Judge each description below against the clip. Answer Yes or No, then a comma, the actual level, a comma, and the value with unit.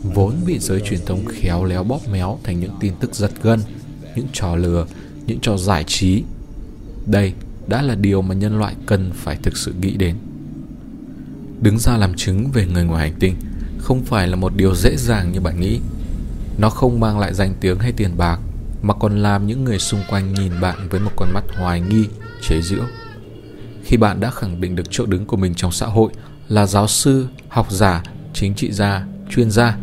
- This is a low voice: Yes, low, 100 Hz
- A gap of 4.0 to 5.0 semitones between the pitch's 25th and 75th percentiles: No, average, 3.4 semitones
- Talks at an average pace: Yes, average, 205 wpm